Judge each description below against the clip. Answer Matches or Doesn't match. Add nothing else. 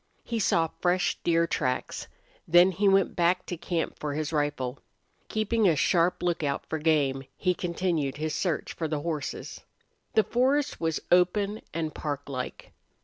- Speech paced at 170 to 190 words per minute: Doesn't match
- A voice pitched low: Doesn't match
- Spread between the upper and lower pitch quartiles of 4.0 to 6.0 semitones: Doesn't match